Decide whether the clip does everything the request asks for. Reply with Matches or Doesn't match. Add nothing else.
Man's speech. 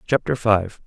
Matches